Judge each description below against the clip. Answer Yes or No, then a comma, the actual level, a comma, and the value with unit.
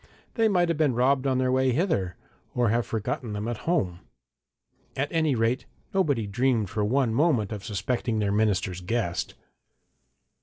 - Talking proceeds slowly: No, average, 160 wpm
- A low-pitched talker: Yes, low, 120 Hz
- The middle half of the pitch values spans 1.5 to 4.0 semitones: No, average, 4.9 semitones